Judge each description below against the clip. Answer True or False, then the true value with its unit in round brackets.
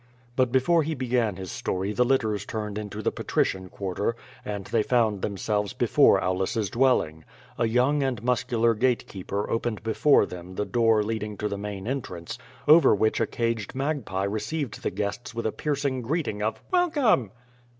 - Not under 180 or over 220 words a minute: False (170 wpm)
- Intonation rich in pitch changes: False (4.0 semitones)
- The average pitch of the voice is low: True (110 Hz)